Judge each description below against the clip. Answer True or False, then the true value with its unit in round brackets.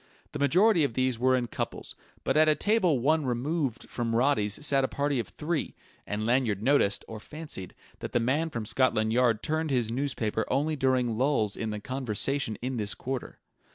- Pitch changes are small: False (4.3 semitones)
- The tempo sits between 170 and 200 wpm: True (190 wpm)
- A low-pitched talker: True (130 Hz)